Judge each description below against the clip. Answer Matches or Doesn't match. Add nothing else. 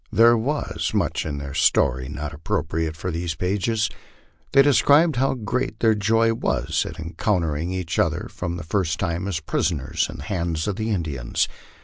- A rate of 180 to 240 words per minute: Doesn't match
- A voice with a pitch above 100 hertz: Doesn't match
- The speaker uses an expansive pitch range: Matches